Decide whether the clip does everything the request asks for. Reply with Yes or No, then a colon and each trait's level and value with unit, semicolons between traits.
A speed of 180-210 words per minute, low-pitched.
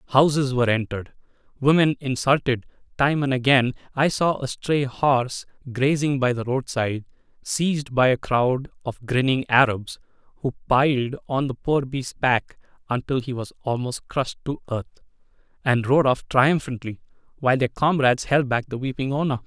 No: average, 155 wpm; low, 130 Hz